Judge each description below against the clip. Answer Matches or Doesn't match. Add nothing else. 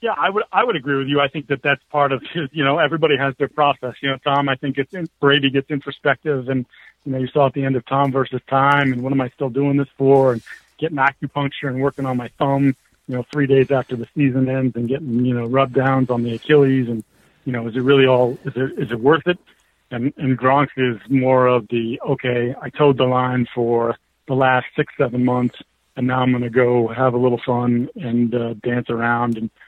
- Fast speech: Matches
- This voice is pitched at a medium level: Doesn't match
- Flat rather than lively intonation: Matches